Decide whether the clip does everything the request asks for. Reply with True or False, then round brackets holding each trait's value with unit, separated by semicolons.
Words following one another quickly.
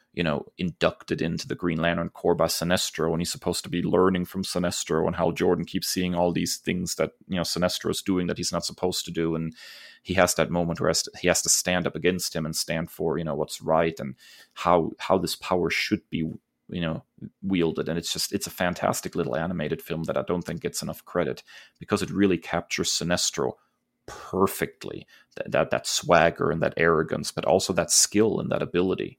True (215 wpm)